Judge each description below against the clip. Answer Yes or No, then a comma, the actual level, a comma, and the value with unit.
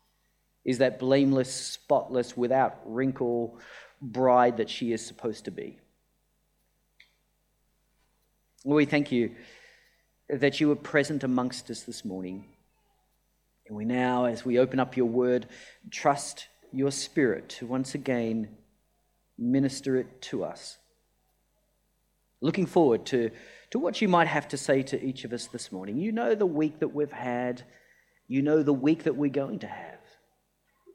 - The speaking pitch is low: Yes, low, 130 Hz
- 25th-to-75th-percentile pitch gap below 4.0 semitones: Yes, average, 2.8 semitones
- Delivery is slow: No, average, 145 wpm